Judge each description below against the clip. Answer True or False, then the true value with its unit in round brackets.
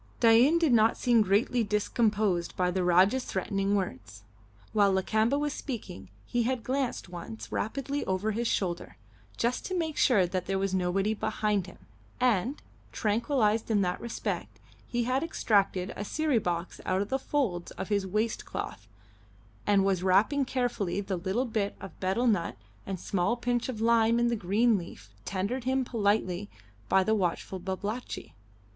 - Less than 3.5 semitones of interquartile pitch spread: False (4.2 semitones)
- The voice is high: True (210 Hz)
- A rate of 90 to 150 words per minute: False (165 wpm)